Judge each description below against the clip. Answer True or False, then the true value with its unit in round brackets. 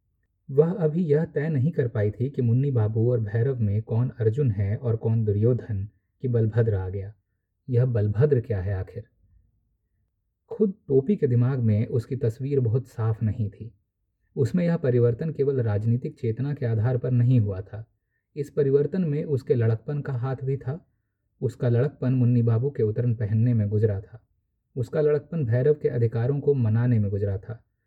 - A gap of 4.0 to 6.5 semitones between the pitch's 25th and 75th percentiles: True (4.3 semitones)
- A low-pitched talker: True (120 Hz)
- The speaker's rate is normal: True (175 wpm)